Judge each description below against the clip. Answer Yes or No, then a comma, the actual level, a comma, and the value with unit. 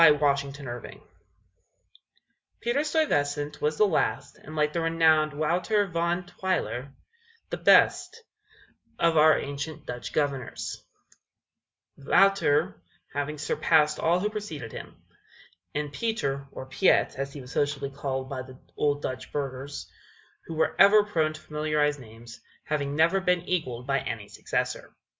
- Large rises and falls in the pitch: No, average, 3.4 semitones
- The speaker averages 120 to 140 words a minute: Yes, slow, 135 wpm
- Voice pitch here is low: No, medium, 150 Hz